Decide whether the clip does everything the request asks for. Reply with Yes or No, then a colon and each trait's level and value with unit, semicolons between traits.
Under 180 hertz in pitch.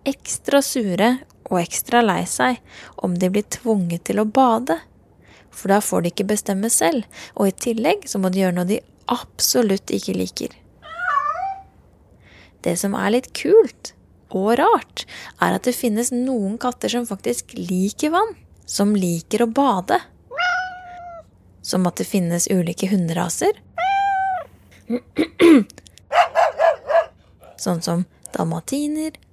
No: high, 225 Hz